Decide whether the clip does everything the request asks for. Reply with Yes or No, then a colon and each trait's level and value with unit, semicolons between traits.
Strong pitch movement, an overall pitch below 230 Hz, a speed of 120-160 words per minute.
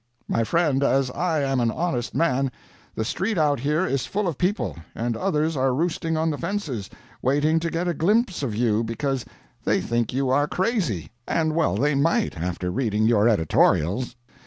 No: wide, 5.9 semitones; medium, 140 Hz; average, 180 wpm